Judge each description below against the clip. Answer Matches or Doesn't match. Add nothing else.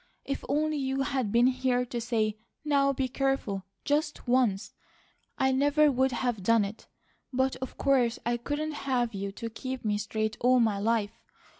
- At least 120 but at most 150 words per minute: Doesn't match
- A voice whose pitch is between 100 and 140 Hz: Doesn't match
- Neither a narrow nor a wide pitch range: Matches